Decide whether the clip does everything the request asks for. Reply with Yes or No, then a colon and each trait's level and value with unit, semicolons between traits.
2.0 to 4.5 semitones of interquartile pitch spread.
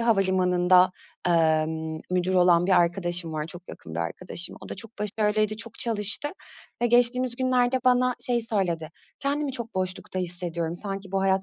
No: average, 4.9 semitones